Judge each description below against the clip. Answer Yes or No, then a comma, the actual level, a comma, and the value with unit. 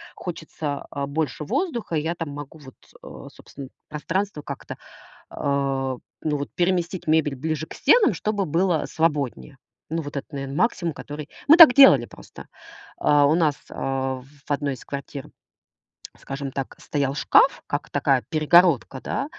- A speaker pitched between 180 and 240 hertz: No, medium, 150 Hz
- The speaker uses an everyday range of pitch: Yes, average, 3.3 semitones